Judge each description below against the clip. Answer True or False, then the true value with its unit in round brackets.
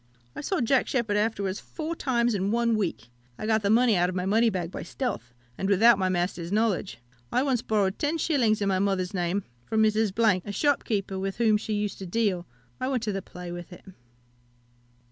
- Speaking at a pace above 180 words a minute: True (200 wpm)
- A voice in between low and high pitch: False (210 Hz)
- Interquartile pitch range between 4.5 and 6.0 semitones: False (3.6 semitones)